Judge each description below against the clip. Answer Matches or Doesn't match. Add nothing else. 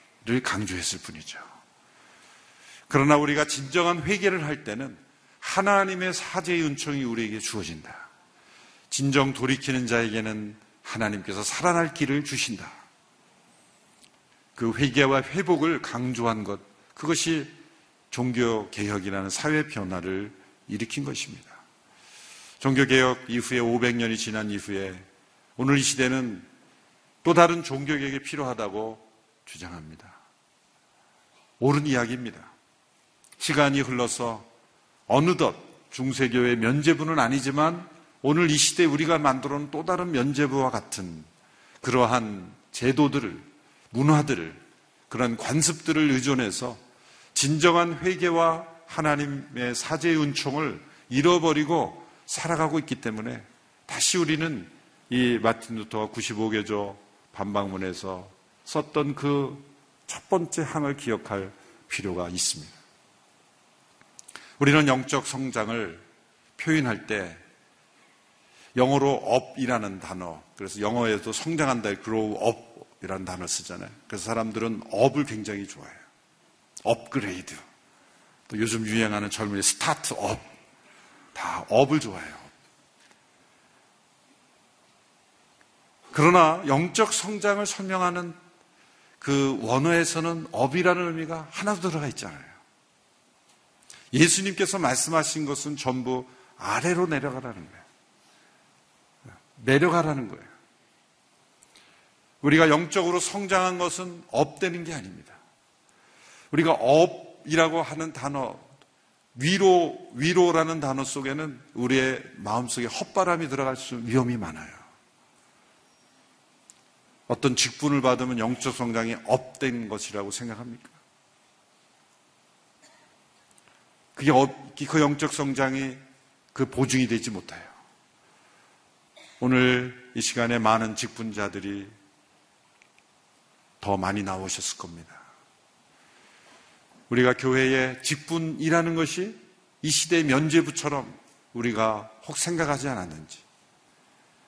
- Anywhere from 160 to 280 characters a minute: Matches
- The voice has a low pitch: Matches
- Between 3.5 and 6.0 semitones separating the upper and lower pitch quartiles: Matches